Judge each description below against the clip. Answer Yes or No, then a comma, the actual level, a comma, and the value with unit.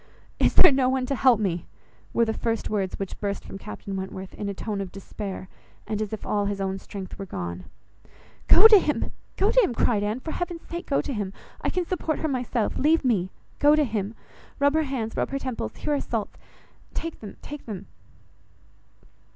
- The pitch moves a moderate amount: No, wide, 6.2 semitones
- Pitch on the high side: Yes, high, 225 Hz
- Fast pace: Yes, fast, 210 wpm